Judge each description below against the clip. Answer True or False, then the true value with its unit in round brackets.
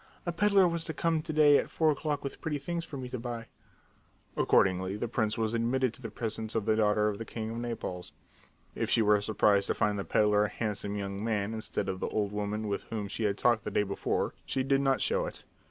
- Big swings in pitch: False (4.6 semitones)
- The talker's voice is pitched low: True (110 Hz)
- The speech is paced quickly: True (240 wpm)